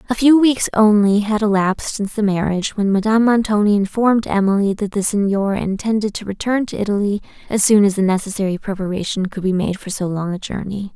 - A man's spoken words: No, female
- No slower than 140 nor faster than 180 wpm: No, average, 195 wpm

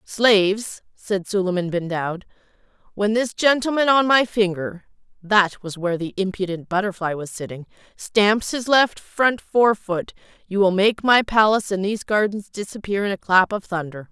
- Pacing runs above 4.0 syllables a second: No, 3.9 syllables/s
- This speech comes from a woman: Yes, female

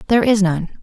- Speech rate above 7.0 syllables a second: Yes, 7.7 syllables/s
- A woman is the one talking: Yes, female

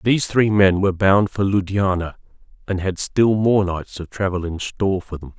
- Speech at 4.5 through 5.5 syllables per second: Yes, 5.1 syllables/s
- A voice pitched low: Yes, very low, 95 Hz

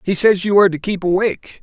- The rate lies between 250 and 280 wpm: Yes, fast, 260 wpm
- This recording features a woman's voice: No, male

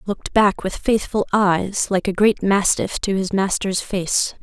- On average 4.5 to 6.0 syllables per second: No, 4.1 syllables/s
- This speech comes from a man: No, female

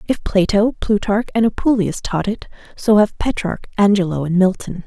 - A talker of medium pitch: No, high, 200 Hz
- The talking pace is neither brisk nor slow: Yes, average, 160 wpm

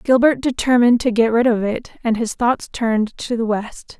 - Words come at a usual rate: No, fast, 210 wpm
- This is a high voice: Yes, high, 235 Hz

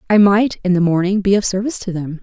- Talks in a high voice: Yes, high, 195 Hz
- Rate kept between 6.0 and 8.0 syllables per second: Yes, 6.5 syllables/s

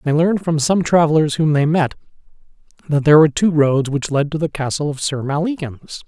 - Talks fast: Yes, fast, 210 wpm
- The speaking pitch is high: No, medium, 155 Hz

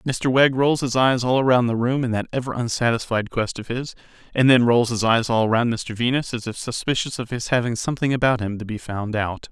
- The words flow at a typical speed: No, fast, 240 wpm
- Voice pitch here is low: Yes, low, 120 Hz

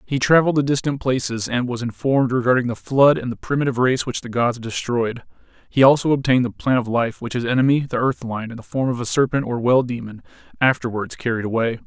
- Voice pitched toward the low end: Yes, low, 125 Hz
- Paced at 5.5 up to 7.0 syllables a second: Yes, 6.2 syllables/s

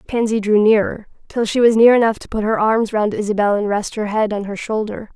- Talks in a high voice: Yes, high, 215 Hz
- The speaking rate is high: Yes, fast, 245 wpm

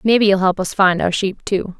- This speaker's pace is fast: Yes, fast, 270 wpm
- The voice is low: No, high, 190 Hz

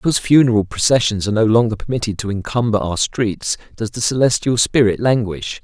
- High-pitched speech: No, low, 110 Hz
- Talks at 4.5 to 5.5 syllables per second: No, 5.9 syllables/s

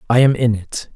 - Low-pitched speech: Yes, low, 120 Hz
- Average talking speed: No, fast, 250 wpm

